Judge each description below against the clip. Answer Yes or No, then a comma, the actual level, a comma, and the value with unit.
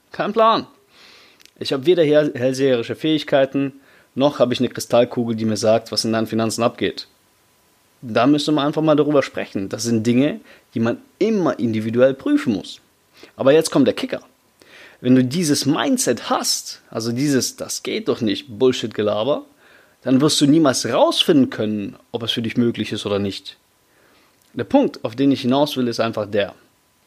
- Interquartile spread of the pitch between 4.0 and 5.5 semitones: Yes, average, 4.5 semitones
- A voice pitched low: Yes, low, 130 Hz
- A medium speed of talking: Yes, average, 170 wpm